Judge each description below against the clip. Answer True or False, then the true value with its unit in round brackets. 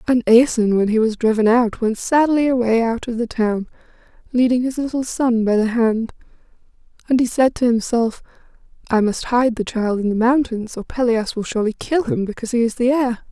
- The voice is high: True (235 Hz)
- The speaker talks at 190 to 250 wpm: True (205 wpm)